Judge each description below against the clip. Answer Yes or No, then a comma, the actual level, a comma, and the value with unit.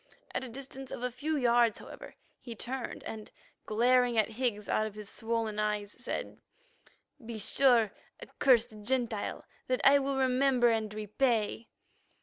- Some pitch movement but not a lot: Yes, average, 3.1 semitones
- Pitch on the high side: Yes, high, 235 Hz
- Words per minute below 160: Yes, average, 145 wpm